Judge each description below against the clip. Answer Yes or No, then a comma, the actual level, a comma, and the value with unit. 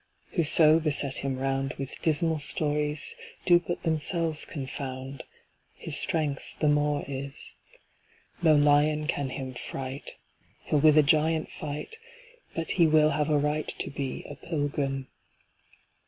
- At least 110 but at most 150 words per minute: Yes, slow, 135 wpm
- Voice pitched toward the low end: No, medium, 150 Hz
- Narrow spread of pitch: Yes, narrow, 2.1 semitones